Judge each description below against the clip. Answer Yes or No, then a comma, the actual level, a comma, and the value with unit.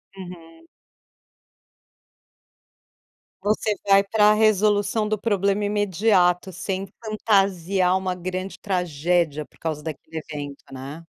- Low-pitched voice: No, medium, 185 Hz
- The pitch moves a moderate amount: Yes, average, 3.8 semitones